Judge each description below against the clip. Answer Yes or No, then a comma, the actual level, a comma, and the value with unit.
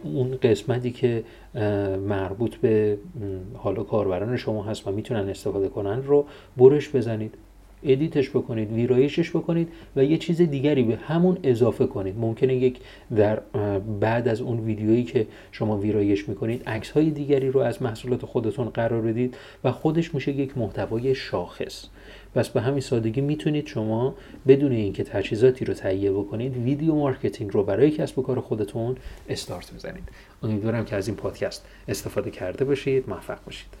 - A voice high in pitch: No, low, 120 Hz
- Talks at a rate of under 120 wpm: No, fast, 155 wpm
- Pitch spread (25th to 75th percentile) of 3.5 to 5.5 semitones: Yes, average, 4.1 semitones